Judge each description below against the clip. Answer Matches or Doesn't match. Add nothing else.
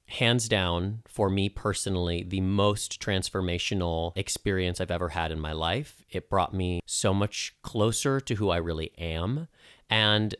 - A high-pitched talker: Doesn't match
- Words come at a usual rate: Matches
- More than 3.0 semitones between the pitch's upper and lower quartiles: Matches